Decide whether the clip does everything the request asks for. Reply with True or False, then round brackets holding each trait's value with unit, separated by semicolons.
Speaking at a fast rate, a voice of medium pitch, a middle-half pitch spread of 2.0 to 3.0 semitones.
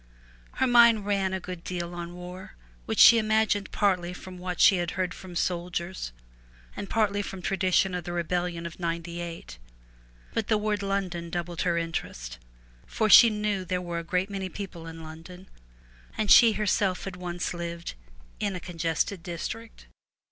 False (165 wpm; 180 Hz; 2.6 semitones)